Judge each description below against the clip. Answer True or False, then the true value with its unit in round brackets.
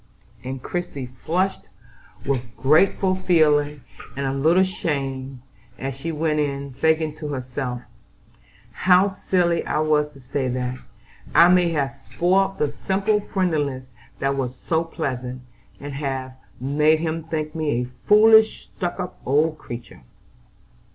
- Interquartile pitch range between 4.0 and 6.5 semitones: True (4.3 semitones)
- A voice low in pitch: False (150 Hz)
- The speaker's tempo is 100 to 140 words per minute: True (135 wpm)